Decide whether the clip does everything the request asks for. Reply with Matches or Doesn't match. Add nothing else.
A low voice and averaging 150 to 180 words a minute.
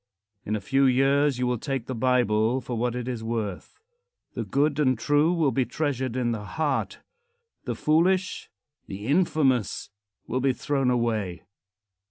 Matches